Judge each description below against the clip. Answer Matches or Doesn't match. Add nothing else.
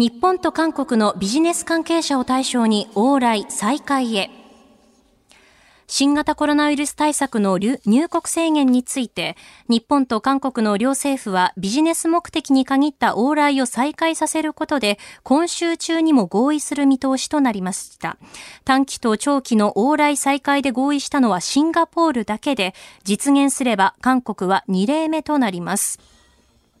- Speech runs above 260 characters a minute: Matches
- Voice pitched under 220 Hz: Doesn't match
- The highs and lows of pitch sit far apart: Doesn't match